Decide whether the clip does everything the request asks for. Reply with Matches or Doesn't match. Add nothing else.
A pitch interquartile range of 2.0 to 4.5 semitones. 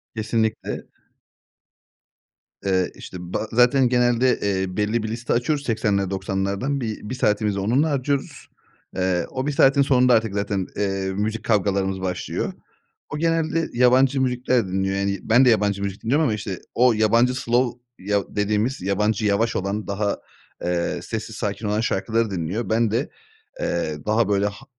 Matches